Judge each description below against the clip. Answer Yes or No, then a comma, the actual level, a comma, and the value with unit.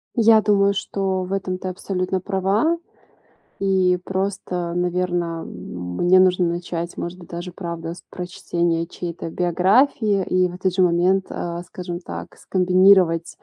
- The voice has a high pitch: No, medium, 180 Hz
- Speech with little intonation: Yes, narrow, 1.8 semitones